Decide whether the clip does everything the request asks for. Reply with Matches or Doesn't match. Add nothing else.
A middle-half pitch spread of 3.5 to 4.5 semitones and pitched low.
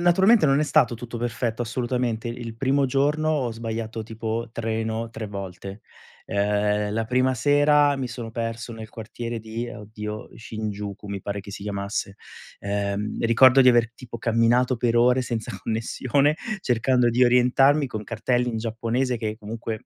Doesn't match